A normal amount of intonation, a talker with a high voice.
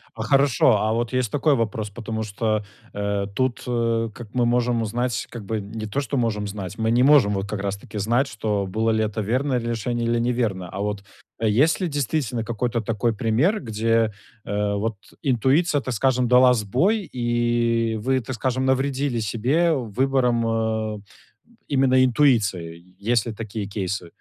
No: average, 3.2 semitones; low, 115 Hz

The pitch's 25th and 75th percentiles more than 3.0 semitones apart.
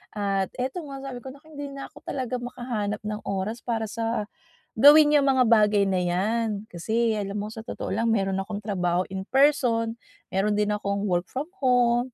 Yes: average, 3.8 semitones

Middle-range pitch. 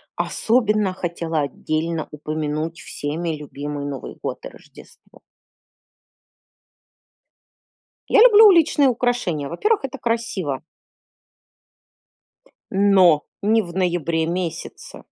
Yes: medium, 175 Hz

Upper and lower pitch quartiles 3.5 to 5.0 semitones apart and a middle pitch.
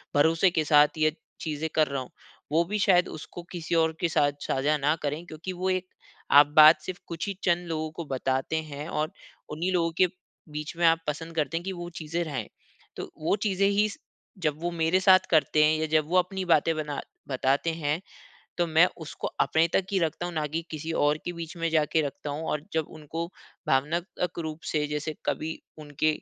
No: narrow, 2.4 semitones; medium, 160 Hz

